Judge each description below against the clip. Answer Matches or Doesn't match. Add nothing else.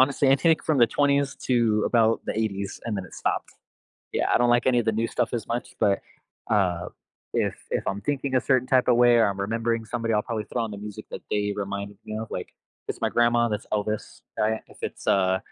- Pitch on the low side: Matches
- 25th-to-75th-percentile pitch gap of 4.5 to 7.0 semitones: Doesn't match